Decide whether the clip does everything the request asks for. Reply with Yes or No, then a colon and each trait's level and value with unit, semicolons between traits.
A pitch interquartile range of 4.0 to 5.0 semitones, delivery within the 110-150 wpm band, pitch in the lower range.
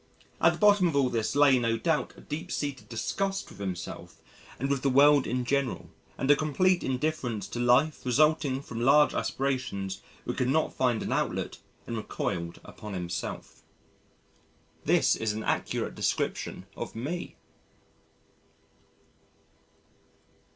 Yes: average, 4.5 semitones; average, 140 wpm; low, 130 Hz